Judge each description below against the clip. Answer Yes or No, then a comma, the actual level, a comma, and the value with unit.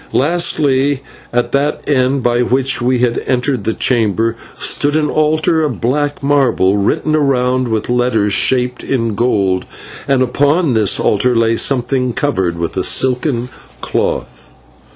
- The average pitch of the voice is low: Yes, low, 125 Hz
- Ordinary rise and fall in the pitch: Yes, average, 3.4 semitones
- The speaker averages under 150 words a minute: Yes, average, 140 wpm